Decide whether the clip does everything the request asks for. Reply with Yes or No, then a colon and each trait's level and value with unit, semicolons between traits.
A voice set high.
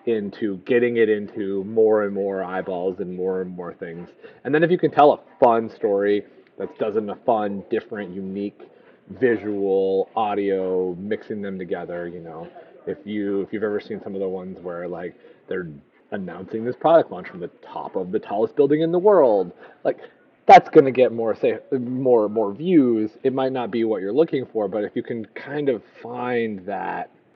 No: low, 105 Hz